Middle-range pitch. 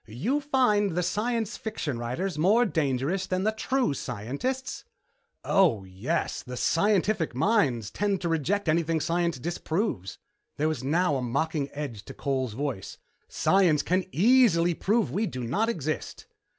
Yes: medium, 170 Hz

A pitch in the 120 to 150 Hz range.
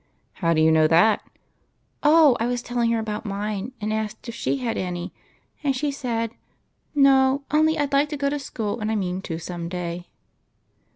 No: high, 225 Hz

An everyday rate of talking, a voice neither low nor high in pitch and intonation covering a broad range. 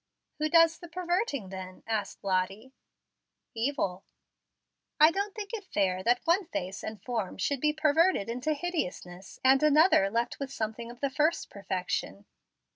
No: average, 150 wpm; very high, 255 Hz; wide, 8.6 semitones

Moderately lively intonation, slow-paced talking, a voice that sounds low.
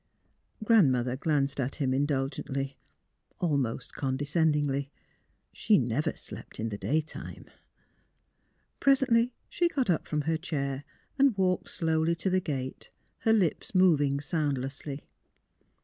No: average, 4.7 semitones; slow, 120 wpm; medium, 150 Hz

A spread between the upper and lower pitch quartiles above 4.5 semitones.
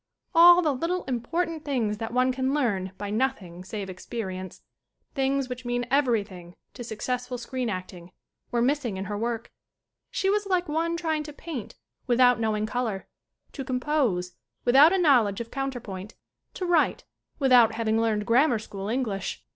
Yes: average, 5.0 semitones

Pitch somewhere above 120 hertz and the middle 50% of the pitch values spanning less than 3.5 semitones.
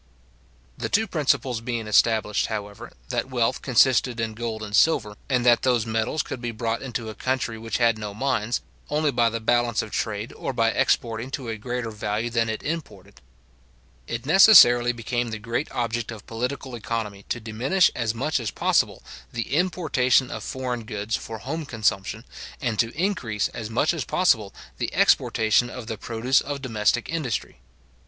No: low, 115 Hz; average, 2.8 semitones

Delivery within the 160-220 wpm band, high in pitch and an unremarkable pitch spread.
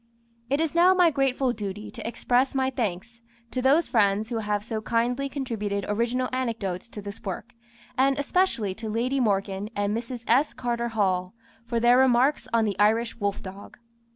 Yes: average, 175 wpm; high, 235 Hz; average, 3.9 semitones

